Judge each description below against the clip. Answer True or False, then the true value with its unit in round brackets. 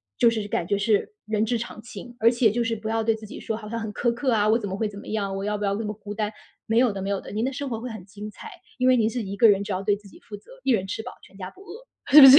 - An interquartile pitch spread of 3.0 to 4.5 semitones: False (2.4 semitones)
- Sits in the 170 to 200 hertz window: False (220 Hz)